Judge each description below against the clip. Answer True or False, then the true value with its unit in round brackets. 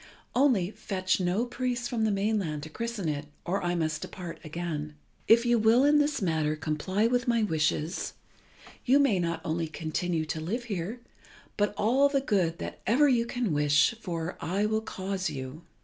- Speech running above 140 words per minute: True (180 wpm)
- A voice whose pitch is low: False (190 Hz)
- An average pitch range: False (6.5 semitones)